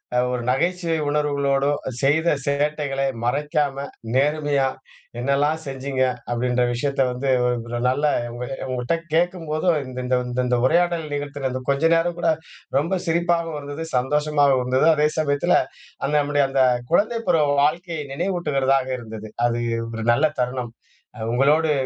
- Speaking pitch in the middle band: Yes, medium, 145 Hz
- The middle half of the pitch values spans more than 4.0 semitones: No, average, 3.2 semitones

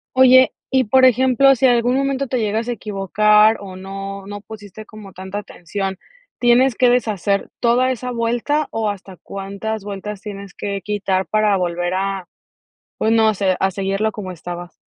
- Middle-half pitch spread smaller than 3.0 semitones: No, average, 3.6 semitones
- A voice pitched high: Yes, high, 210 Hz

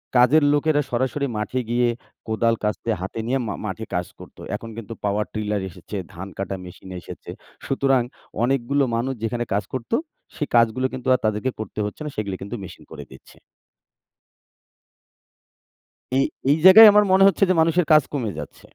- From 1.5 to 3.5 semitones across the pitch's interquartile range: No, average, 4.4 semitones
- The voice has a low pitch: Yes, low, 120 Hz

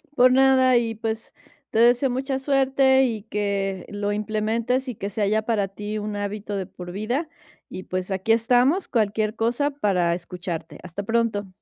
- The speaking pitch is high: Yes, high, 220 Hz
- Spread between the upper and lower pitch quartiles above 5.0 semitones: No, average, 3.7 semitones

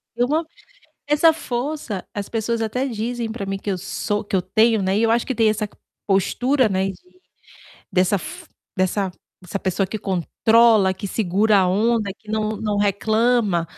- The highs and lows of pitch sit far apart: No, average, 3.4 semitones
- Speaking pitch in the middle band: No, high, 215 Hz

